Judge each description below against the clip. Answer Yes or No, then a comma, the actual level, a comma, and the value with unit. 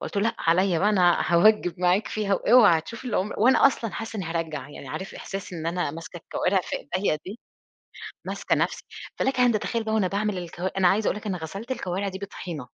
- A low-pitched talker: No, high, 190 Hz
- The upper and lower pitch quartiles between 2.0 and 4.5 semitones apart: Yes, average, 3.7 semitones